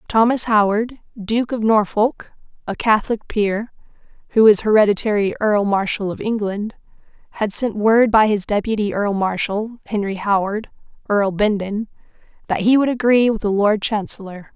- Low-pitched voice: No, high, 210 Hz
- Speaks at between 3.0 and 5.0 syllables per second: Yes, 4.8 syllables/s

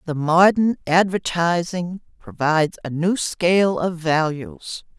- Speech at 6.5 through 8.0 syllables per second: No, 3.9 syllables/s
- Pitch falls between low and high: Yes, medium, 170 Hz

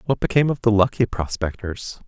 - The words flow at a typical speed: Yes, average, 175 wpm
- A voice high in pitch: No, low, 110 Hz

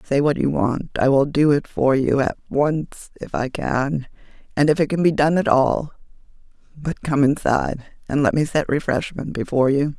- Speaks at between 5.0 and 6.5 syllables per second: Yes, 5.1 syllables/s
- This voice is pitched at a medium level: Yes, medium, 145 Hz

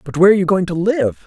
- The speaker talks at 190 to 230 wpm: No, fast, 330 wpm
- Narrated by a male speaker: Yes, male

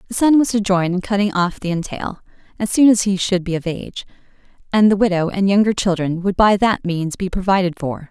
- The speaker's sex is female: Yes, female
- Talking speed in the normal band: No, fast, 230 wpm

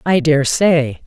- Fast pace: No, average, 170 wpm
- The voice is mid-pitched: Yes, medium, 150 Hz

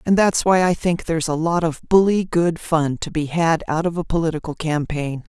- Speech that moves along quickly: Yes, fast, 225 wpm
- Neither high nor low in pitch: Yes, medium, 165 Hz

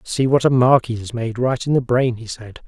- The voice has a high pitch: No, low, 120 Hz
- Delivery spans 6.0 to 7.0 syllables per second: No, 5.1 syllables/s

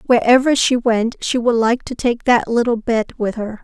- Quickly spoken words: Yes, fast, 215 wpm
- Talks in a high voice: Yes, high, 235 Hz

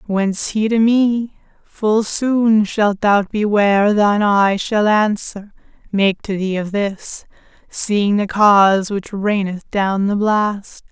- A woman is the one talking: Yes, female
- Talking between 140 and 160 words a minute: Yes, average, 150 wpm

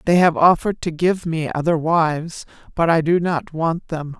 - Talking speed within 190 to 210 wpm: Yes, average, 200 wpm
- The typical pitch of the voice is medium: Yes, medium, 165 Hz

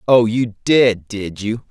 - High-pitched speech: No, low, 110 Hz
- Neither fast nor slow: Yes, average, 175 wpm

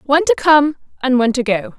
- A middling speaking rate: No, fast, 235 wpm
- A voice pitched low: No, very high, 260 Hz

